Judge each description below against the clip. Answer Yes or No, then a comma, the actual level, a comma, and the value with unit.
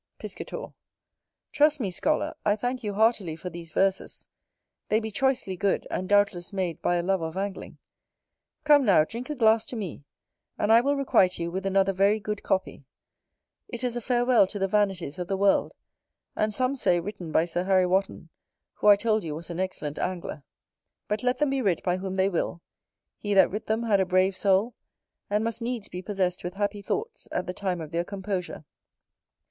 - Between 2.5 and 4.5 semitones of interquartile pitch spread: Yes, average, 3.5 semitones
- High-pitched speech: Yes, high, 195 Hz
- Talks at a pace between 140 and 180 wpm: No, average, 195 wpm